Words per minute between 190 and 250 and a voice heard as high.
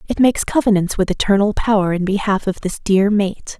Yes: average, 200 wpm; high, 200 Hz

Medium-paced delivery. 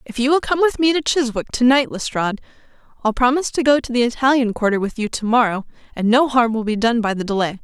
No: fast, 250 wpm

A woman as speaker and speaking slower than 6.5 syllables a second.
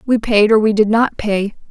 Yes: female; 4.8 syllables/s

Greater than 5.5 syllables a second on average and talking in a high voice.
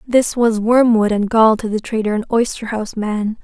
No: 5.0 syllables/s; high, 220 Hz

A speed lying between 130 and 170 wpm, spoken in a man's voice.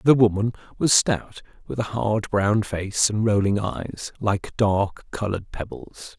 Yes: average, 155 wpm; male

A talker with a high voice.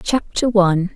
Yes: high, 200 Hz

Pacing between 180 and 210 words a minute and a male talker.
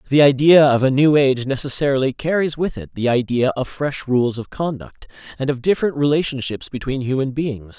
Yes: average, 185 wpm; male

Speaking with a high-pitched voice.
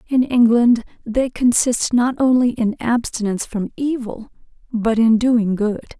Yes: high, 235 Hz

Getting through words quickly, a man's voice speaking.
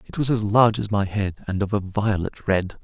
Yes: fast, 255 wpm; male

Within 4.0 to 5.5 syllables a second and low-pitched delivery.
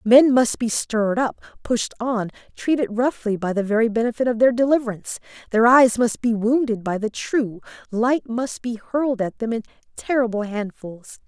No: 5.0 syllables/s; high, 230 Hz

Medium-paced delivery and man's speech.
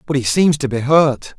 No: fast, 260 wpm; male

